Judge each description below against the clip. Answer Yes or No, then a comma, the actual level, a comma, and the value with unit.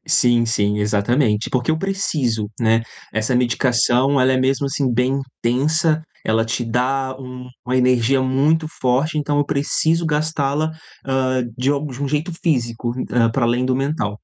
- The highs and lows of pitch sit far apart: No, average, 3.2 semitones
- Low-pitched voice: Yes, low, 130 Hz